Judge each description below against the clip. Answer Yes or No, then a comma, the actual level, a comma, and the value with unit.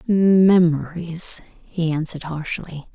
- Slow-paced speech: Yes, slow, 80 wpm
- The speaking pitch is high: No, medium, 170 Hz